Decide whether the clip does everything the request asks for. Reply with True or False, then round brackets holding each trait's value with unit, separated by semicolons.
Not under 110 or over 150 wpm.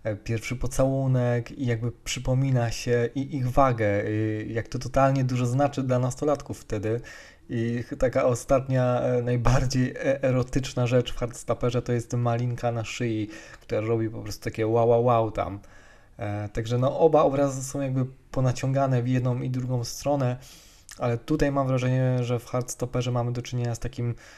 False (160 wpm)